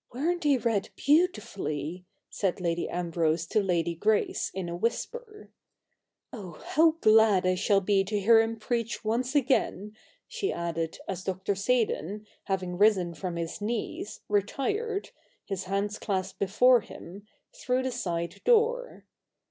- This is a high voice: Yes, high, 205 Hz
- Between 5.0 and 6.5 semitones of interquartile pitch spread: Yes, average, 5.3 semitones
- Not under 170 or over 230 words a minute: No, average, 155 wpm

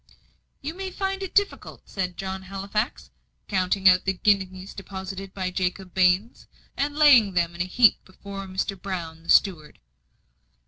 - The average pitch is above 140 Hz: Yes, high, 190 Hz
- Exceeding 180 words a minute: No, average, 150 wpm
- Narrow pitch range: Yes, narrow, 2.2 semitones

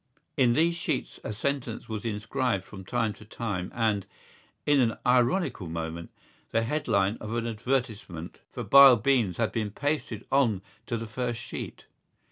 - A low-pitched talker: Yes, low, 115 Hz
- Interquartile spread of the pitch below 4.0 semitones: Yes, average, 3.6 semitones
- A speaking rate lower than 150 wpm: No, average, 155 wpm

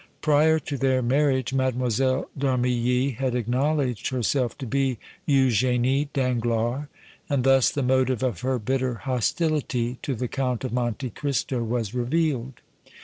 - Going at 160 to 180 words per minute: No, average, 140 wpm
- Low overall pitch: Yes, low, 130 Hz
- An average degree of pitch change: No, narrow, 1.9 semitones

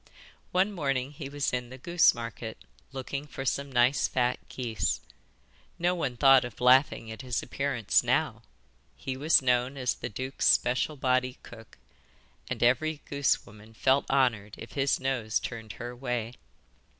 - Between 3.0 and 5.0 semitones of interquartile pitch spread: No, narrow, 2.4 semitones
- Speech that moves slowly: No, average, 155 wpm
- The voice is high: No, low, 130 Hz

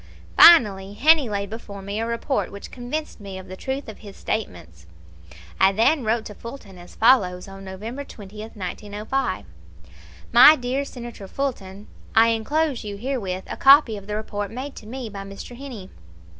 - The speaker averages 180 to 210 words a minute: No, average, 170 wpm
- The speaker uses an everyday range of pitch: Yes, average, 4.5 semitones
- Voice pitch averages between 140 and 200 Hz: No, high, 220 Hz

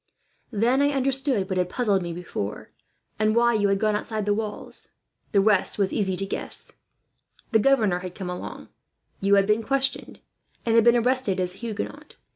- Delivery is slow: No, average, 190 wpm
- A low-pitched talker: No, high, 210 Hz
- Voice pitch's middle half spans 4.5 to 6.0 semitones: No, average, 3.6 semitones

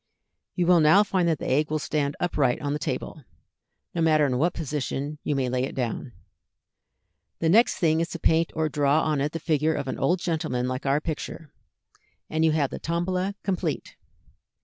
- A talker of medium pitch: Yes, medium, 155 Hz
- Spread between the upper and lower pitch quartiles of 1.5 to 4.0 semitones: Yes, average, 2.8 semitones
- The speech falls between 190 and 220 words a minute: Yes, average, 195 wpm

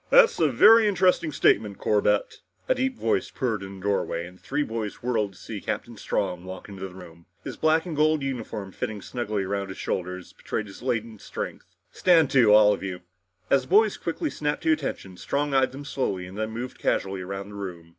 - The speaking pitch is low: Yes, low, 110 Hz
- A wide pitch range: Yes, wide, 7.0 semitones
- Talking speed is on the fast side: Yes, fast, 210 wpm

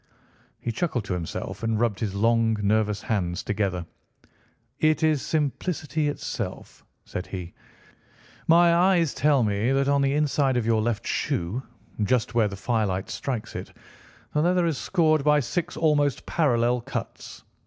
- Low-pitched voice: Yes, low, 120 Hz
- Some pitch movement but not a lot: No, wide, 6.0 semitones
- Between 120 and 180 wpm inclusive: Yes, average, 150 wpm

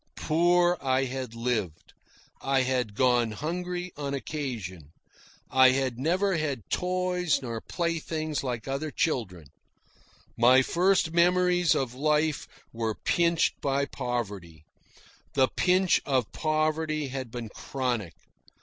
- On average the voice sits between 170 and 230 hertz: No, low, 135 Hz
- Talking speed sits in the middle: No, slow, 115 wpm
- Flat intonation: No, average, 5.3 semitones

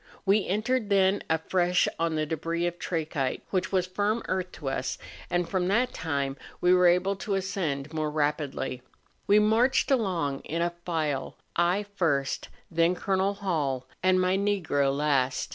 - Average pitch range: Yes, average, 4.2 semitones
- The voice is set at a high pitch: No, medium, 175 Hz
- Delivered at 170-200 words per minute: No, average, 160 wpm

